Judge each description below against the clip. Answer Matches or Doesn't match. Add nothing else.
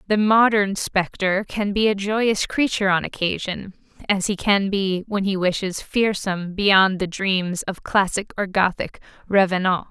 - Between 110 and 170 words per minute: Matches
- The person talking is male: Doesn't match